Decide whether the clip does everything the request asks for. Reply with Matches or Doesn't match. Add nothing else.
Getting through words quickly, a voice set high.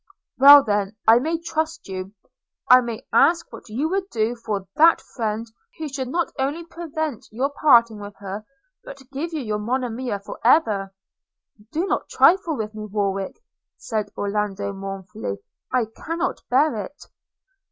Doesn't match